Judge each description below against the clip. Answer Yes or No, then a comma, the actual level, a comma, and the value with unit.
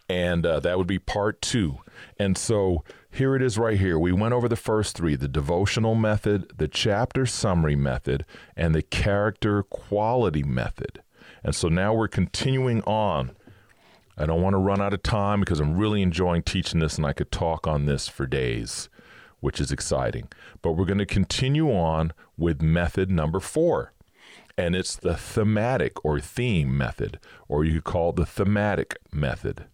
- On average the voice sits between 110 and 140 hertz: No, very low, 95 Hz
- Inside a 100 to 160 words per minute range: No, average, 175 wpm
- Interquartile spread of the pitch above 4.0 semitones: Yes, average, 4.7 semitones